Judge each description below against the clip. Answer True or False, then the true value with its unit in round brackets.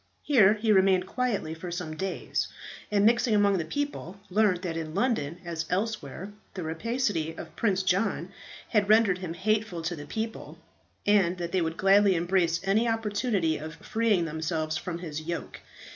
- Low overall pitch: False (190 Hz)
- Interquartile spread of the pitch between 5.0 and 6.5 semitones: False (4.4 semitones)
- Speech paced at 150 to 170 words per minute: True (165 wpm)